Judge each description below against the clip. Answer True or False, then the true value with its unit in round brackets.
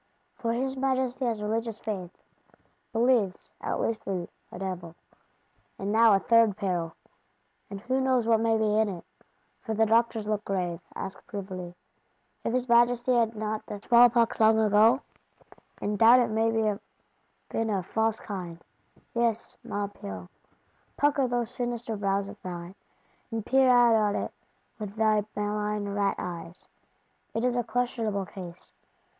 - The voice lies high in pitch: True (220 Hz)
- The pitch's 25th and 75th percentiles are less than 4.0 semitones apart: True (2.9 semitones)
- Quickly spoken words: False (150 wpm)